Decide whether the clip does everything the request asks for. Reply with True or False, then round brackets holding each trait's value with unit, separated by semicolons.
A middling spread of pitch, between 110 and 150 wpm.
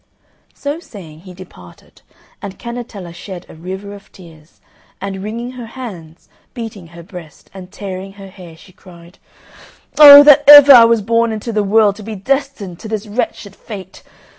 False (4.2 semitones; 165 wpm)